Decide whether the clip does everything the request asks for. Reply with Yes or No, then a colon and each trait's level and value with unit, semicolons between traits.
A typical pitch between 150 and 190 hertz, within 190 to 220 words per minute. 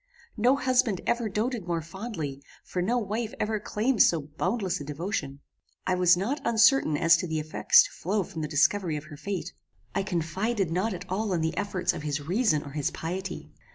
Yes: medium, 185 Hz; average, 195 wpm